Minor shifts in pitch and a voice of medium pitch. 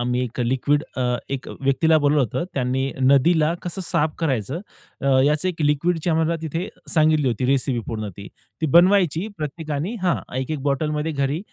No: average, 3.5 semitones; medium, 150 Hz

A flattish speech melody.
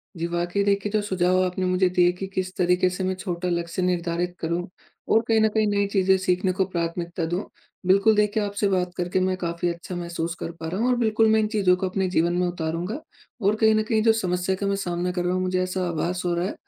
Yes: narrow, 2.2 semitones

